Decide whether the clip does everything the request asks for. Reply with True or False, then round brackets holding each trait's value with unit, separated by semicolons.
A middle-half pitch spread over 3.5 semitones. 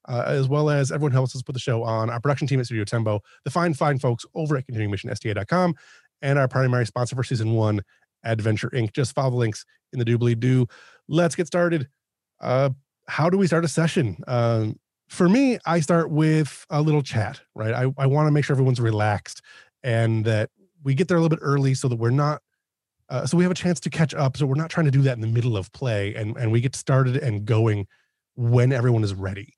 True (4.5 semitones)